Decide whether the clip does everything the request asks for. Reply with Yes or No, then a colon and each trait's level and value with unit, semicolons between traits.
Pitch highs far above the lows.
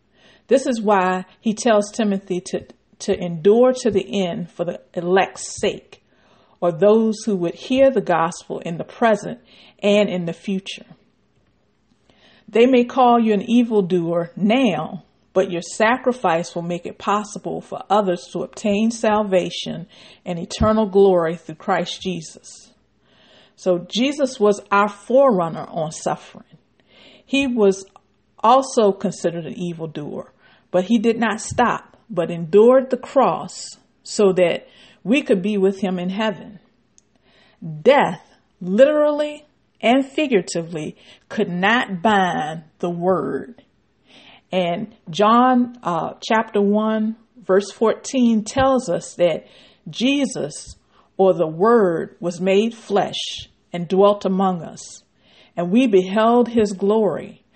No: average, 3.8 semitones